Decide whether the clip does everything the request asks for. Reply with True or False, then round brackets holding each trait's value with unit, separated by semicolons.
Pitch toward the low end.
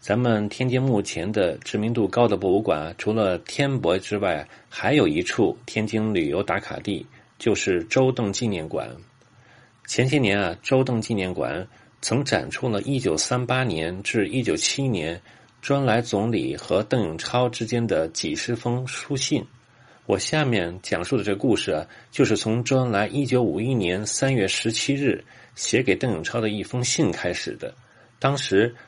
True (120 Hz)